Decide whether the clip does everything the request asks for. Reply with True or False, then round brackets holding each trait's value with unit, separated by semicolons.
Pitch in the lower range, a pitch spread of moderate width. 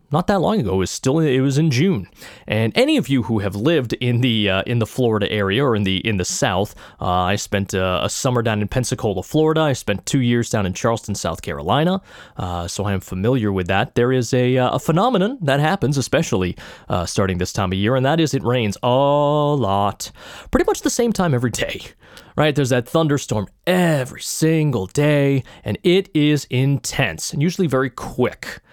False (125 Hz; 6.1 semitones)